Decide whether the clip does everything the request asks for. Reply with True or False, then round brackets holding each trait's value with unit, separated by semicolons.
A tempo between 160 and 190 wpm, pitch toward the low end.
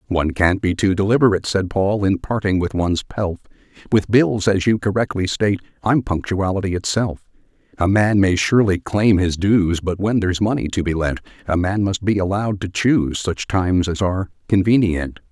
True (185 wpm; 95 Hz)